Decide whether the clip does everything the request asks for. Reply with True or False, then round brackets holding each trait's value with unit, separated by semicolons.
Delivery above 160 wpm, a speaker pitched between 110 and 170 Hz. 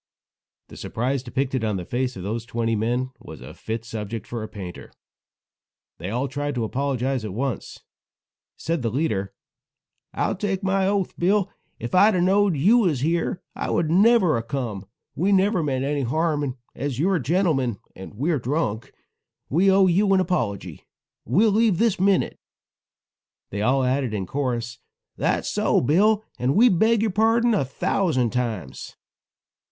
True (170 wpm; 140 Hz)